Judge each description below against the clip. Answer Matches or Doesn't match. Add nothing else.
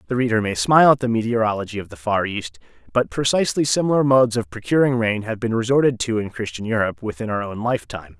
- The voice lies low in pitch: Matches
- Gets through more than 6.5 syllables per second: Matches